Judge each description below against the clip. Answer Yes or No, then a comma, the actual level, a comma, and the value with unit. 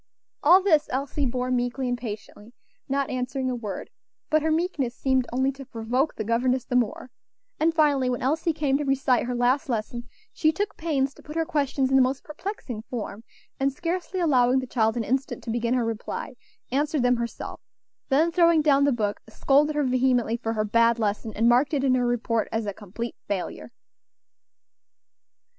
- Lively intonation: No, average, 3.5 semitones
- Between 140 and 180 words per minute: No, average, 190 wpm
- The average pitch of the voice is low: No, very high, 255 Hz